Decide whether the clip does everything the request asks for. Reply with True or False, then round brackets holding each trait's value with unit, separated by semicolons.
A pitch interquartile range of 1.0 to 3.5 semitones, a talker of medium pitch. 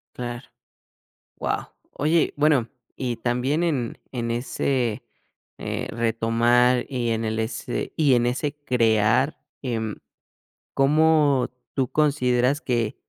False (3.1 semitones; 125 Hz)